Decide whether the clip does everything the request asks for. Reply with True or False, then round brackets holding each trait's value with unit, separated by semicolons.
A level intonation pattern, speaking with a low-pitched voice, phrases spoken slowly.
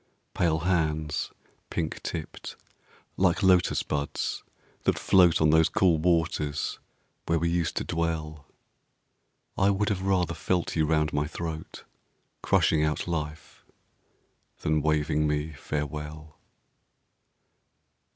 True (2.0 semitones; 80 Hz; 110 wpm)